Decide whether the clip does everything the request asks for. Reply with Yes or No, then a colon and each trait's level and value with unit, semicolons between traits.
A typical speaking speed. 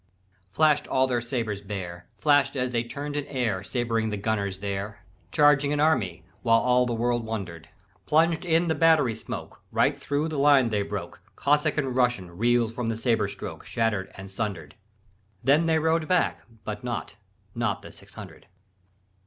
Yes: average, 170 wpm